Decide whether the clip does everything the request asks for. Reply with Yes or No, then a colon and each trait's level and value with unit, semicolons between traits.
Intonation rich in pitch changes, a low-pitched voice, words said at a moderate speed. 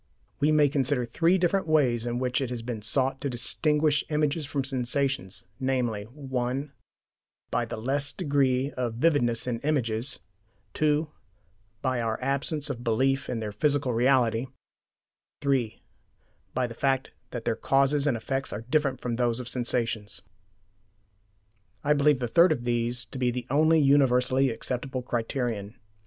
No: average, 3.1 semitones; low, 130 Hz; average, 150 wpm